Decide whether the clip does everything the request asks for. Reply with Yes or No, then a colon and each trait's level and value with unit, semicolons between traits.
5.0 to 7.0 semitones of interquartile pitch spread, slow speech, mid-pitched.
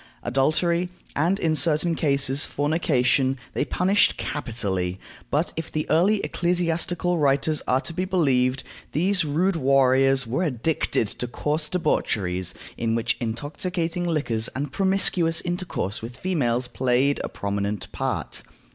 Yes: average, 5.3 semitones; slow, 130 wpm; medium, 145 Hz